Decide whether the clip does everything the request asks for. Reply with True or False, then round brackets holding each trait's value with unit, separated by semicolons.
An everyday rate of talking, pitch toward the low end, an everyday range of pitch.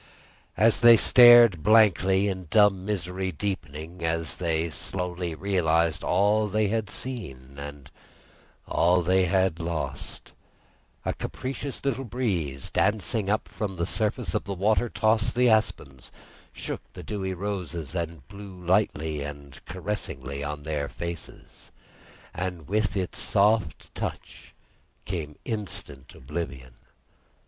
False (120 wpm; 90 Hz; 4.8 semitones)